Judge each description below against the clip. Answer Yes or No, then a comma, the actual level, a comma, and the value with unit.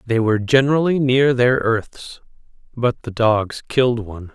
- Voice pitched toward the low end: Yes, low, 120 Hz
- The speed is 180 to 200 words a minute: No, average, 150 wpm